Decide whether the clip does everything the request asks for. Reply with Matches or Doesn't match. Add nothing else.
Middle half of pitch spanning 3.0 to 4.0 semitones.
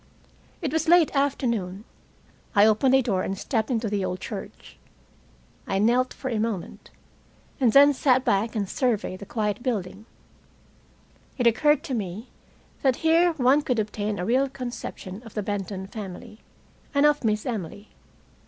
Doesn't match